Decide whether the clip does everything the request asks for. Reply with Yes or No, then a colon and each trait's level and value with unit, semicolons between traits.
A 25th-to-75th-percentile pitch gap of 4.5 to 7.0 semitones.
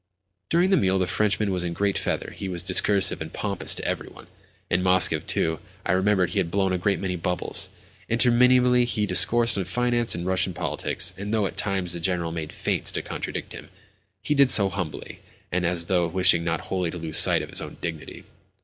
No: average, 3.2 semitones